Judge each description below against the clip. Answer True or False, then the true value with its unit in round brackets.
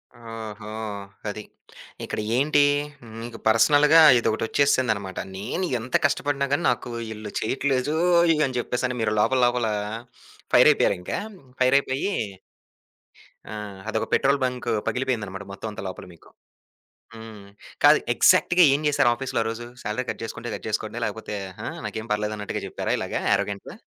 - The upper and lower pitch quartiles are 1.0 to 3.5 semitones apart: False (4.3 semitones)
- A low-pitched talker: True (120 Hz)